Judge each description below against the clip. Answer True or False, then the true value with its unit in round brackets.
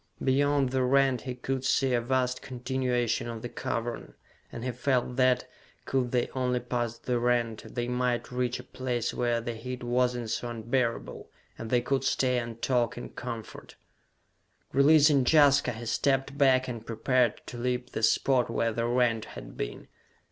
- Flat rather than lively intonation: True (1.6 semitones)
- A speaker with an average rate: True (170 wpm)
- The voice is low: True (125 Hz)